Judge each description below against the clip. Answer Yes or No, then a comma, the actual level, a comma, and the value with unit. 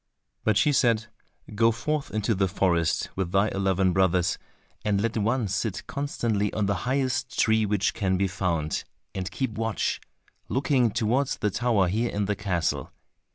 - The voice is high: No, low, 105 Hz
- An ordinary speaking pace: Yes, average, 160 wpm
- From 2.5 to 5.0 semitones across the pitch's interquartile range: Yes, average, 3.5 semitones